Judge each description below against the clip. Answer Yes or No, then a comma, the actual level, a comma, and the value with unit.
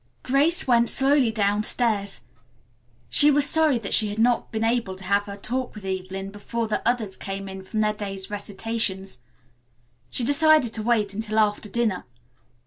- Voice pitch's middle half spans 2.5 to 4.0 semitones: Yes, average, 3.2 semitones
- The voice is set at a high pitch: Yes, high, 215 Hz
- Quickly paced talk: No, average, 165 wpm